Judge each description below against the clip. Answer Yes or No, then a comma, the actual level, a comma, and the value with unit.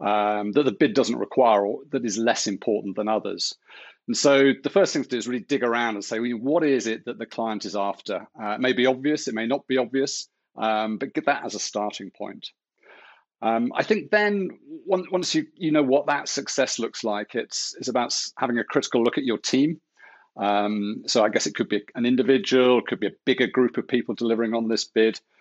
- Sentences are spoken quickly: Yes, fast, 230 wpm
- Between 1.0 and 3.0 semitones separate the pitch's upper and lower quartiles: No, average, 4.1 semitones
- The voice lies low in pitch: Yes, low, 125 Hz